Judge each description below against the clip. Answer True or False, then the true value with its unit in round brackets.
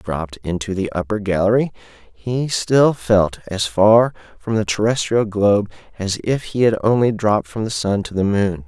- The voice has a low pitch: True (105 Hz)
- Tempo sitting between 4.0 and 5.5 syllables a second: True (5.1 syllables/s)